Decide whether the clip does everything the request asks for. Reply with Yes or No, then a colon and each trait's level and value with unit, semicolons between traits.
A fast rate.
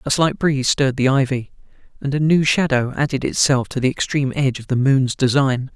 Yes: fast, 210 wpm